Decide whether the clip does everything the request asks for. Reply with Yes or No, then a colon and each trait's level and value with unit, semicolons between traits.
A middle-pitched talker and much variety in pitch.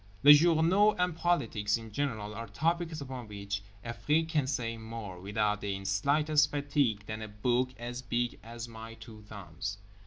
No: low, 115 Hz; wide, 5.7 semitones